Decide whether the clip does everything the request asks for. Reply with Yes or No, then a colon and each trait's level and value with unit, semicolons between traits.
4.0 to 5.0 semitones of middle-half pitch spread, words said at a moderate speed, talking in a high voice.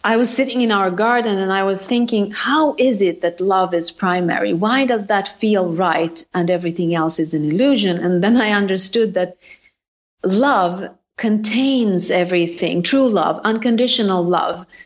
Yes: average, 4.6 semitones; average, 160 wpm; high, 195 Hz